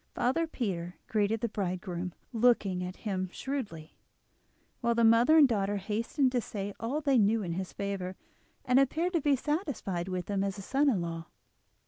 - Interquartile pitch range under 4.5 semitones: No, wide, 5.5 semitones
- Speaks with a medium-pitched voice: No, high, 210 Hz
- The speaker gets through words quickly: No, average, 175 wpm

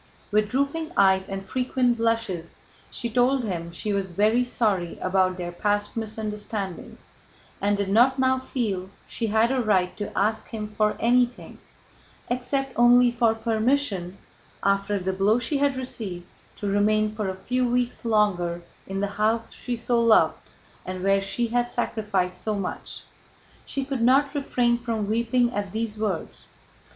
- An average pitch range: Yes, average, 3.6 semitones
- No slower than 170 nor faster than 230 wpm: No, average, 155 wpm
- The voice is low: No, high, 220 Hz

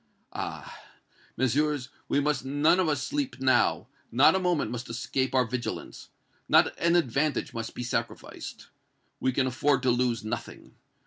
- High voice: No, low, 130 Hz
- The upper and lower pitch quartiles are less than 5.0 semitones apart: Yes, average, 3.1 semitones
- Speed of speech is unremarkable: Yes, average, 150 wpm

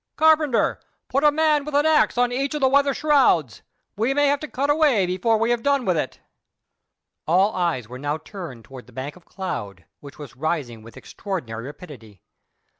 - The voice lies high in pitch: Yes, high, 195 Hz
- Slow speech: No, average, 190 wpm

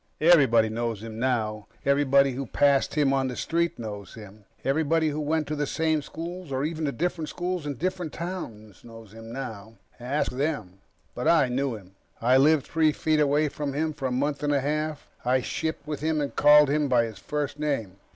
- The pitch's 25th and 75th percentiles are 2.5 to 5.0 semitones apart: Yes, average, 4.5 semitones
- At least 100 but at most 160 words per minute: No, average, 200 wpm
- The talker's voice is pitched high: No, medium, 140 Hz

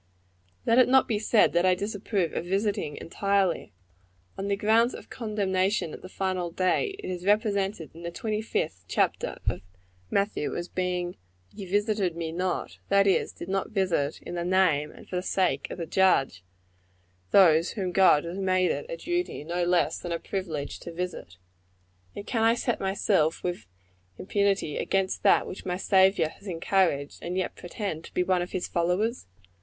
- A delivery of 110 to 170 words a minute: No, average, 180 wpm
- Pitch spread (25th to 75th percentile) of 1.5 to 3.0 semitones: Yes, average, 2.7 semitones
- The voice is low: No, medium, 185 Hz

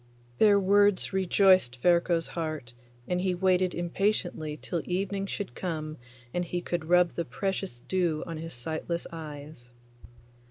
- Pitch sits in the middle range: Yes, medium, 175 Hz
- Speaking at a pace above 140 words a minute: No, slow, 135 wpm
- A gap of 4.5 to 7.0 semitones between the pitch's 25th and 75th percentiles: No, average, 3.0 semitones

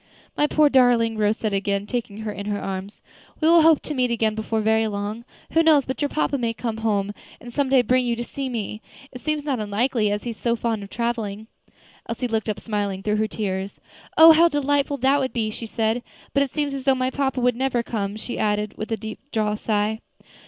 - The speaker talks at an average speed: No, fast, 230 wpm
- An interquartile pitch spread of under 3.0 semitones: No, average, 3.9 semitones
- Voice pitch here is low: No, high, 230 Hz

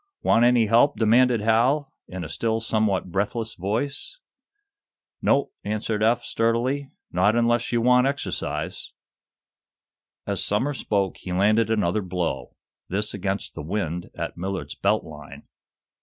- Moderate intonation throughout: Yes, average, 3.5 semitones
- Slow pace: Yes, slow, 130 wpm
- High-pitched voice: No, low, 110 Hz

